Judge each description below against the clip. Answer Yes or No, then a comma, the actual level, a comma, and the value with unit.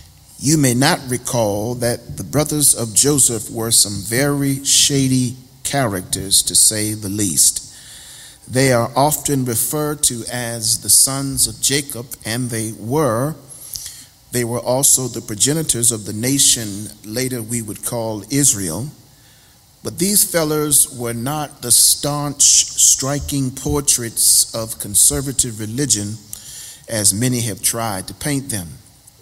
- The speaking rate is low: Yes, slow, 130 wpm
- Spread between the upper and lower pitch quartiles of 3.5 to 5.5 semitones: Yes, average, 3.9 semitones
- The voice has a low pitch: Yes, low, 125 Hz